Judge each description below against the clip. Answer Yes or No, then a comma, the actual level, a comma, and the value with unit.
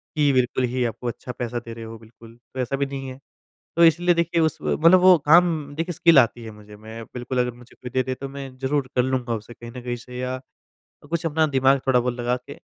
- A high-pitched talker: No, low, 130 Hz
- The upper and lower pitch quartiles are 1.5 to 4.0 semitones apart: Yes, average, 3.5 semitones